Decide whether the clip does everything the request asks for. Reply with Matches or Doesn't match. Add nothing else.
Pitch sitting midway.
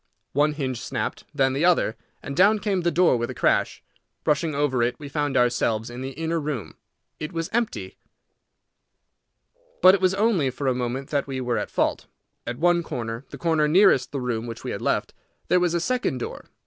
Matches